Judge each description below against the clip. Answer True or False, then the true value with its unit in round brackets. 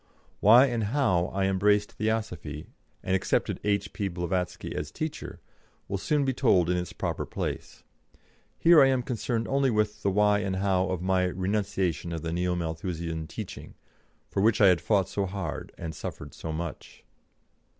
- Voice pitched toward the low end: True (95 Hz)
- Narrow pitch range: False (3.5 semitones)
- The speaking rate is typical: True (165 wpm)